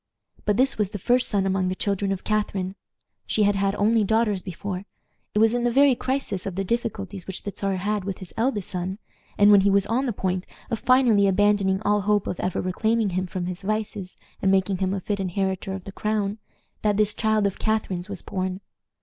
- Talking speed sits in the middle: No, fast, 220 wpm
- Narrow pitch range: Yes, narrow, 2.1 semitones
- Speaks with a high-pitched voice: Yes, high, 200 Hz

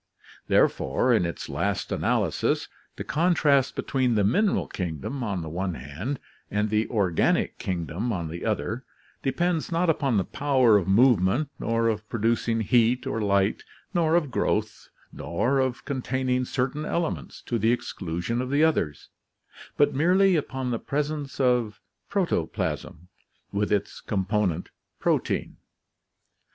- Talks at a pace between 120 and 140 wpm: Yes, slow, 135 wpm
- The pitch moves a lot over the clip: Yes, wide, 5.9 semitones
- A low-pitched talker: Yes, low, 120 Hz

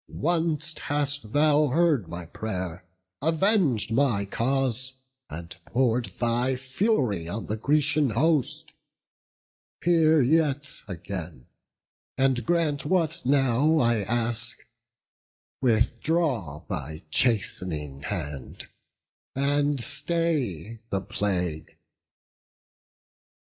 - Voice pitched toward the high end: No, low, 130 Hz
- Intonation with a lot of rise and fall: Yes, wide, 6.5 semitones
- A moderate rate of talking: No, slow, 85 wpm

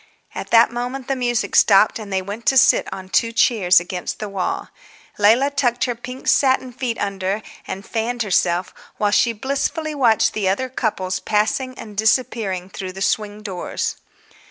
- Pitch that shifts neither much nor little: Yes, average, 4.1 semitones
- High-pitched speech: Yes, high, 220 Hz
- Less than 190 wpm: Yes, average, 170 wpm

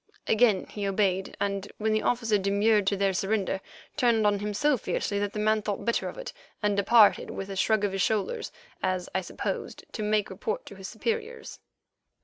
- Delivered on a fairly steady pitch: Yes, narrow, 2.1 semitones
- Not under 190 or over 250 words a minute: Yes, average, 195 wpm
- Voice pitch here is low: No, high, 210 Hz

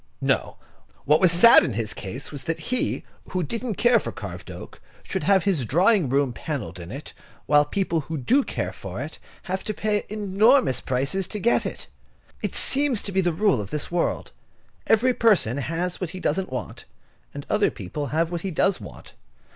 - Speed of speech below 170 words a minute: No, average, 195 wpm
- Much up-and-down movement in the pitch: Yes, wide, 6.6 semitones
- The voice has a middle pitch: Yes, medium, 175 Hz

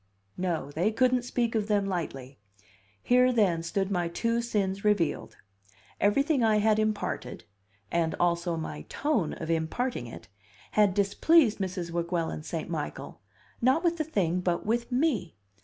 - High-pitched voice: Yes, high, 200 Hz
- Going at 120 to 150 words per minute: Yes, average, 145 wpm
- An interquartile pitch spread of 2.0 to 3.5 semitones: No, wide, 5.6 semitones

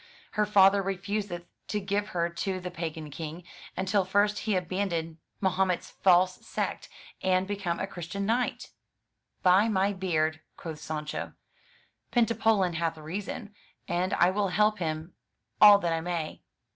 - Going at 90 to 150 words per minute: Yes, average, 140 wpm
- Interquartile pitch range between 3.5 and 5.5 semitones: No, average, 3.0 semitones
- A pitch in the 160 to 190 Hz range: Yes, medium, 185 Hz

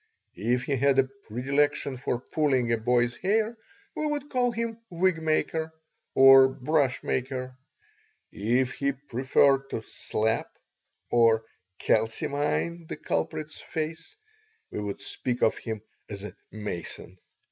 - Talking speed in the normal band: No, slow, 125 wpm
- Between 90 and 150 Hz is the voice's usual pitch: Yes, low, 135 Hz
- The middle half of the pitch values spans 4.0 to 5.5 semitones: Yes, average, 5.2 semitones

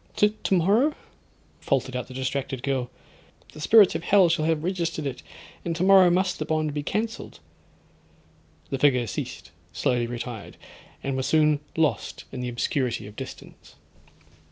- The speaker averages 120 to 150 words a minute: Yes, average, 140 wpm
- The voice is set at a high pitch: No, medium, 150 Hz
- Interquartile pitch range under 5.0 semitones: No, wide, 5.6 semitones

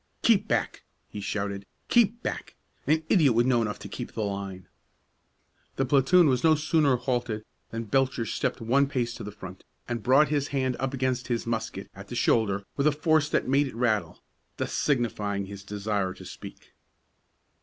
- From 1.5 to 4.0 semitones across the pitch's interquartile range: No, average, 5.0 semitones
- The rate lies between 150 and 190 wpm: Yes, average, 180 wpm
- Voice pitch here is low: Yes, low, 125 Hz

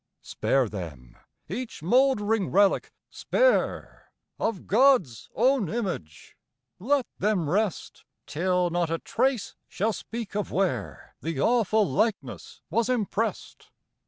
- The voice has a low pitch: No, high, 205 Hz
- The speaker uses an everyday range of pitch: No, wide, 5.7 semitones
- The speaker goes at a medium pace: No, slow, 110 wpm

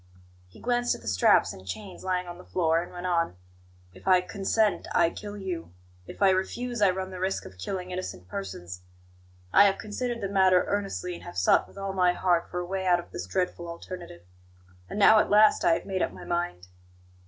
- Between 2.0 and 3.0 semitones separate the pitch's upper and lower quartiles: Yes, average, 2.7 semitones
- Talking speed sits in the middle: No, fast, 215 wpm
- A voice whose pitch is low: No, medium, 180 Hz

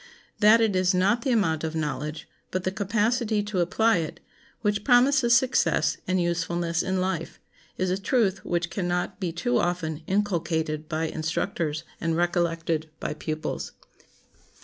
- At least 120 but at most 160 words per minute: Yes, average, 150 wpm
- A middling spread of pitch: Yes, average, 4.2 semitones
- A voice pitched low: No, medium, 180 Hz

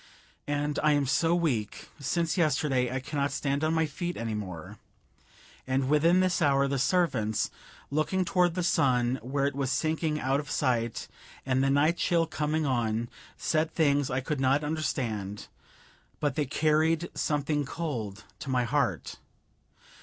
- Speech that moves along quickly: No, average, 155 wpm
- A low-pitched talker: No, medium, 145 Hz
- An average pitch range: Yes, average, 3.4 semitones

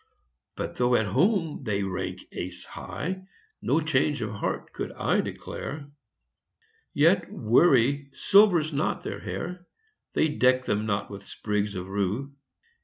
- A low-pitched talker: Yes, low, 130 Hz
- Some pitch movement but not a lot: No, wide, 7.3 semitones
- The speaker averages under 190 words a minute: Yes, slow, 135 wpm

